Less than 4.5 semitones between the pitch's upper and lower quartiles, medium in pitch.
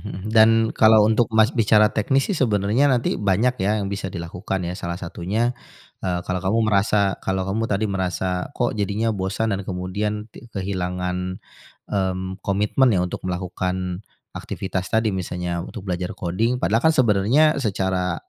No: average, 3.3 semitones; low, 100 Hz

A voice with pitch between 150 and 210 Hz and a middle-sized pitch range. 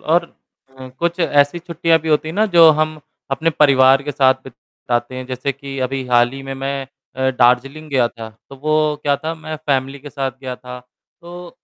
No: medium, 140 Hz; average, 3.1 semitones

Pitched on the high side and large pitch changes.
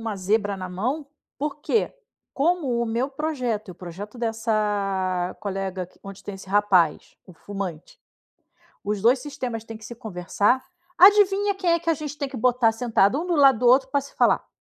Yes: high, 225 Hz; wide, 5.9 semitones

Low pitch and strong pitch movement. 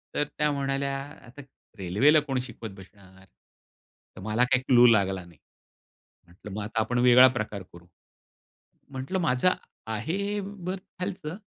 Yes: low, 125 Hz; wide, 6.2 semitones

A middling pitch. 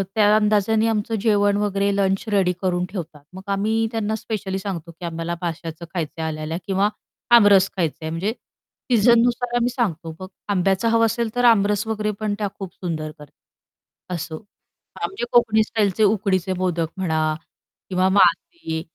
No: high, 195 Hz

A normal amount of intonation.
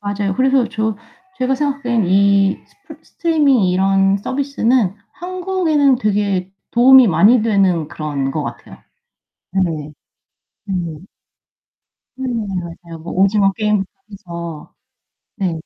No: wide, 5.9 semitones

